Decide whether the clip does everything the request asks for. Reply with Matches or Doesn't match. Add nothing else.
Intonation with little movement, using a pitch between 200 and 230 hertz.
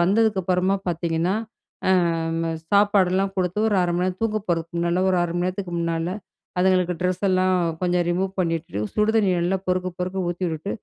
Doesn't match